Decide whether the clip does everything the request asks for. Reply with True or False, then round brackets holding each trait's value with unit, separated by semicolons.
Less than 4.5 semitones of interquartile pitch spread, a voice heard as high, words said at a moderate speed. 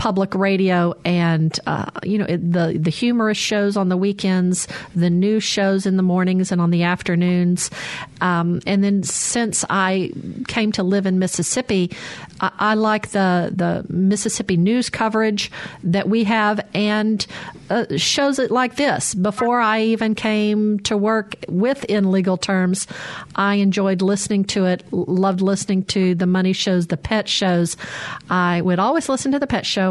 True (2.9 semitones; 195 Hz; 165 wpm)